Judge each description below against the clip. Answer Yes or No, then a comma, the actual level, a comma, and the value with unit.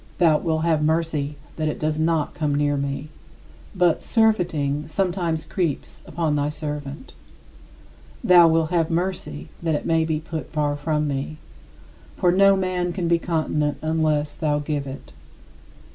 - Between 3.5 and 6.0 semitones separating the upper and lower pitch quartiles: No, narrow, 2.4 semitones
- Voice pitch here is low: No, medium, 155 Hz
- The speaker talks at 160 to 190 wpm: No, average, 150 wpm